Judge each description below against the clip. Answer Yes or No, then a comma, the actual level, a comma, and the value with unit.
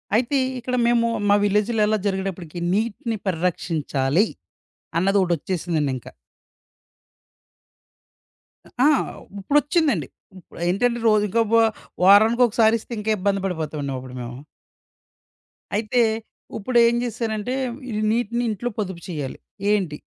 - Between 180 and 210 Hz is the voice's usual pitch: Yes, high, 205 Hz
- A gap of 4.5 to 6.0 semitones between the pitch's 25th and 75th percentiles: Yes, average, 4.9 semitones